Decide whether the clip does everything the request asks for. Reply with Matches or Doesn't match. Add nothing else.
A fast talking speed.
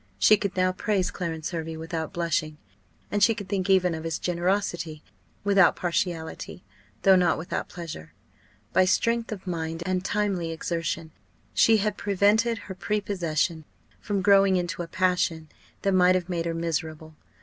Doesn't match